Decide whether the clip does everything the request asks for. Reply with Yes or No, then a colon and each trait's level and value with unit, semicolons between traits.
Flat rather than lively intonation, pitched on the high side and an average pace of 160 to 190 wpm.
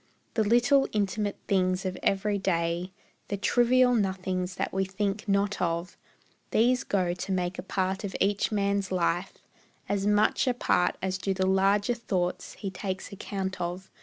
Yes: narrow, 1.9 semitones; high, 195 Hz; average, 165 wpm